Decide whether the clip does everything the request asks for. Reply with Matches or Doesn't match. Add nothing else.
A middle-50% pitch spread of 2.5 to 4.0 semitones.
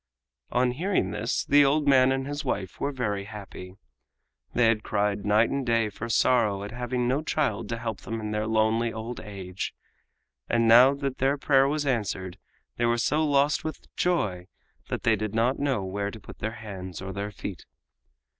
Doesn't match